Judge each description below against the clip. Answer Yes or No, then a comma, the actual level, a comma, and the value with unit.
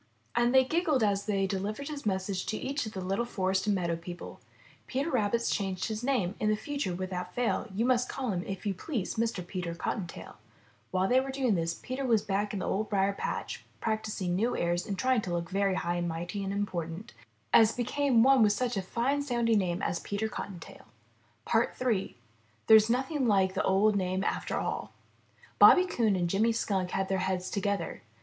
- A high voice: Yes, high, 205 Hz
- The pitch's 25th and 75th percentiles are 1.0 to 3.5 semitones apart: No, average, 4.2 semitones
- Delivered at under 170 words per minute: No, average, 200 wpm